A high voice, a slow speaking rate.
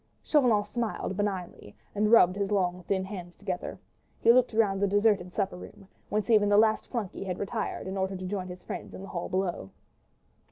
No: high, 195 Hz; average, 195 wpm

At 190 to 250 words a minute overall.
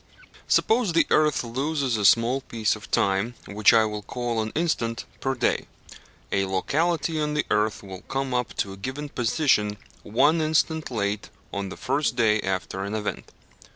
No: average, 170 wpm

